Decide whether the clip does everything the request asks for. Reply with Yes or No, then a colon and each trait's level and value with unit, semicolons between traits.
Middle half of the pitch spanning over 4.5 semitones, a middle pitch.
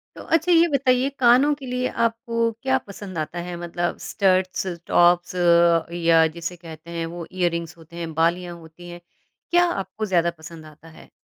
Yes: wide, 5.6 semitones; medium, 175 Hz